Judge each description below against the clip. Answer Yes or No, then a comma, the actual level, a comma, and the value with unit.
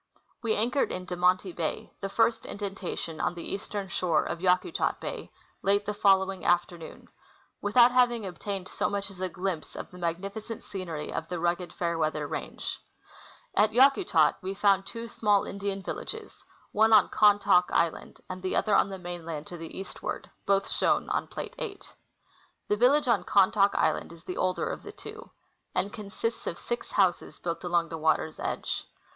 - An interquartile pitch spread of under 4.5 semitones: Yes, average, 2.9 semitones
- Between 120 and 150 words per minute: No, average, 175 wpm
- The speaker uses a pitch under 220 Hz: Yes, high, 190 Hz